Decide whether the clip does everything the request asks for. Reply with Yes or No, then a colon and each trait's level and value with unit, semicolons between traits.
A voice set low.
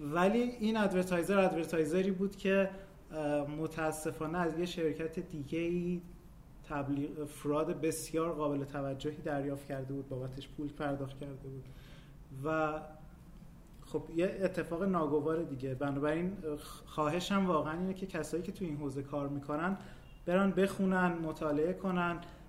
No: medium, 160 Hz